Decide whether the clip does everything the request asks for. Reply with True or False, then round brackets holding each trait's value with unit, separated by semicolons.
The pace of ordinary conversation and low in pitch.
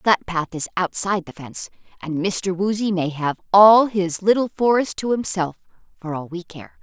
False (185 wpm; 185 Hz)